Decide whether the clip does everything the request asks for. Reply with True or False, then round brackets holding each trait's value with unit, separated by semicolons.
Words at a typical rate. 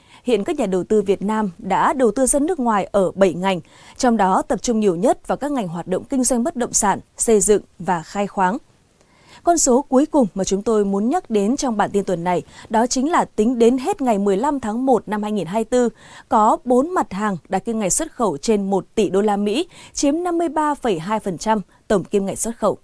True (225 wpm)